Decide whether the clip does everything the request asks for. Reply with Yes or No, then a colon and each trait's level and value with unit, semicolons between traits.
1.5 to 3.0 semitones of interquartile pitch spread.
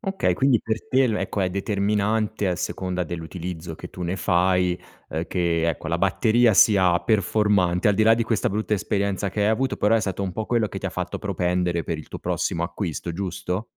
No: average, 3.4 semitones